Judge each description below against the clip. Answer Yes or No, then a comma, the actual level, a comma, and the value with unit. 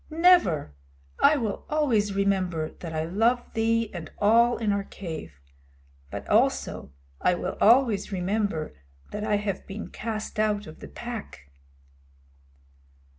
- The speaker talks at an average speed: No, slow, 130 wpm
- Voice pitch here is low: No, high, 205 Hz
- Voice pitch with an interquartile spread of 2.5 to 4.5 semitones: Yes, average, 4.1 semitones